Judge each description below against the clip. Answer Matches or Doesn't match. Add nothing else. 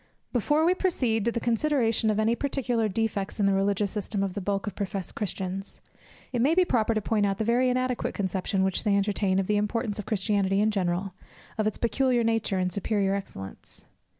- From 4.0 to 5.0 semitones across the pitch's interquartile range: Doesn't match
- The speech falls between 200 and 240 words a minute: Matches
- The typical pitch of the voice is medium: Doesn't match